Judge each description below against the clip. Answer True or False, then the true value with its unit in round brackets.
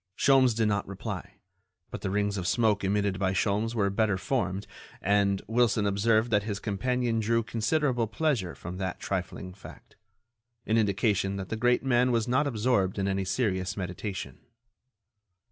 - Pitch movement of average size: True (3.1 semitones)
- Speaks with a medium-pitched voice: False (105 Hz)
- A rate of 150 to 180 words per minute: True (155 wpm)